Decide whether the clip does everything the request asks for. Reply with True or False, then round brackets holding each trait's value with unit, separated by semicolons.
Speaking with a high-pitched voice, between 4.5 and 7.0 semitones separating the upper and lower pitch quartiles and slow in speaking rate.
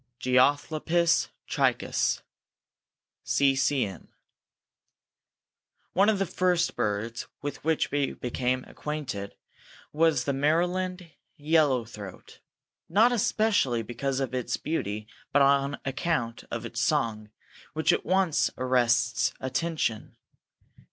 False (140 Hz; 5.2 semitones; 105 wpm)